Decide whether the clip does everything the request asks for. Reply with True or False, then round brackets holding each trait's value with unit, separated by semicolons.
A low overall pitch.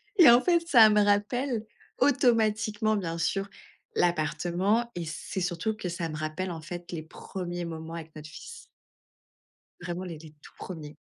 False (180 Hz)